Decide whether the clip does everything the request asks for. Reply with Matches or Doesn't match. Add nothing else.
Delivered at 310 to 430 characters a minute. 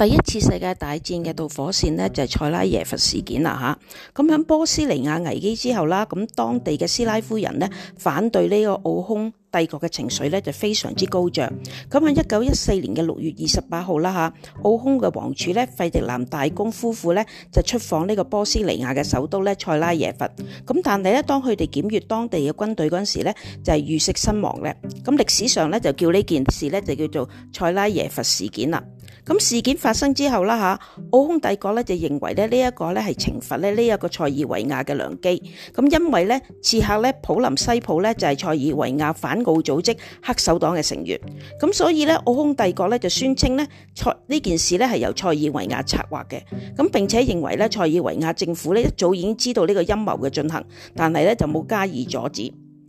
Matches